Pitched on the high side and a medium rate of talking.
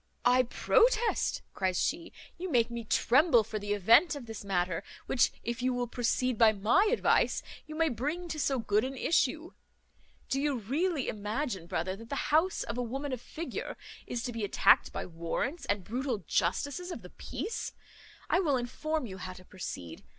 Yes: high, 245 Hz; average, 185 wpm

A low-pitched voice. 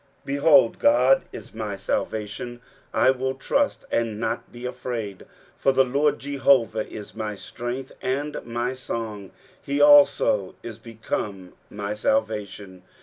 Yes: low, 120 Hz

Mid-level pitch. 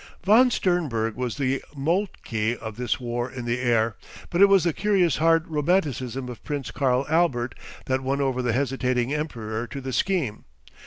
No: low, 130 Hz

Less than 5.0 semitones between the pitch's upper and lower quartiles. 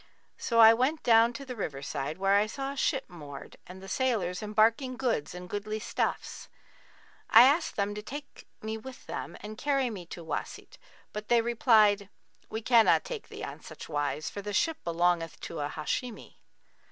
No: wide, 5.4 semitones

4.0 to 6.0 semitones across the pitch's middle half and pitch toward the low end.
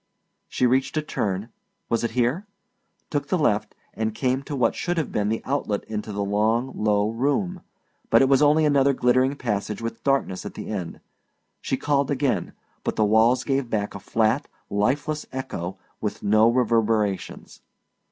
Yes: average, 4.5 semitones; low, 120 Hz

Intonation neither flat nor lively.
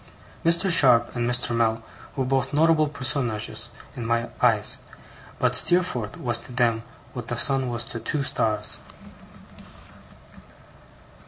Yes: average, 3.2 semitones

